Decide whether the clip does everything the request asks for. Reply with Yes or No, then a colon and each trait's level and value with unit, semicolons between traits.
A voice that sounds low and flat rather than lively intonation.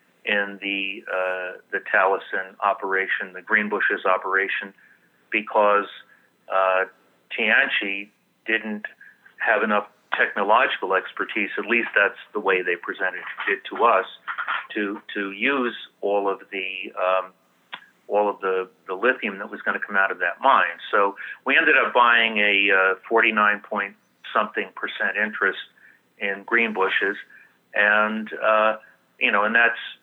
Yes: low, 100 Hz; narrow, 2.1 semitones